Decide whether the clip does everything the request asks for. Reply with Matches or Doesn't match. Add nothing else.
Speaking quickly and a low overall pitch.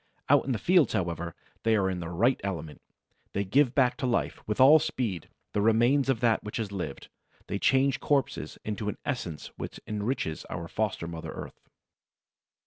Doesn't match